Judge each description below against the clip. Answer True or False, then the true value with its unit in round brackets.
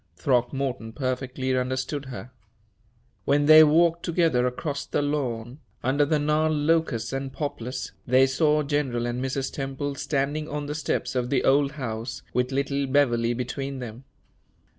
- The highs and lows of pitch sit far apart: False (2.6 semitones)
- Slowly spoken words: False (145 wpm)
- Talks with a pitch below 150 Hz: True (135 Hz)